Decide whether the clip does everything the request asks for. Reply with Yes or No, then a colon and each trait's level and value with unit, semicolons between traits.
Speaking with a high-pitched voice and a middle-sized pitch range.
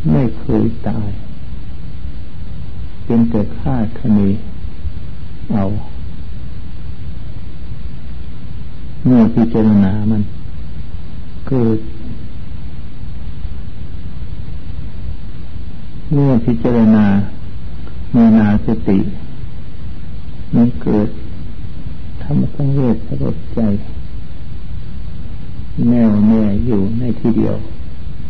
No: low, 100 Hz; average, 4.8 semitones